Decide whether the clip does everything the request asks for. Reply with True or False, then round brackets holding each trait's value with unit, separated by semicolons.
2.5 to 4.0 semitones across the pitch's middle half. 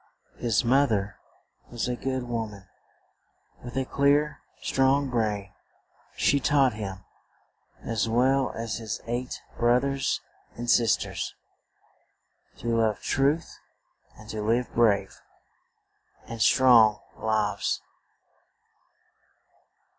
True (3.4 semitones)